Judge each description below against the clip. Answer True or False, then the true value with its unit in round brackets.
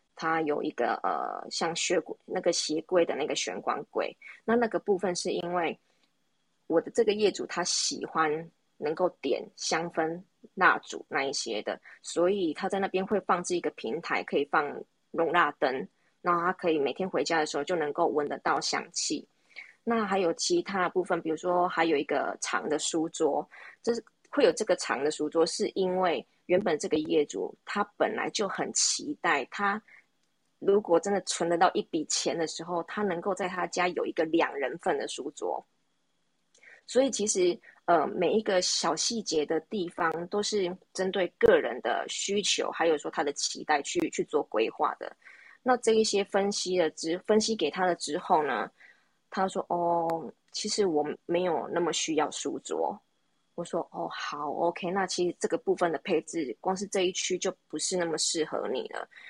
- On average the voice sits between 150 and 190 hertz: True (185 Hz)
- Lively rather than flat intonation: False (4.2 semitones)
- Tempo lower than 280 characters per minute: True (260 characters per minute)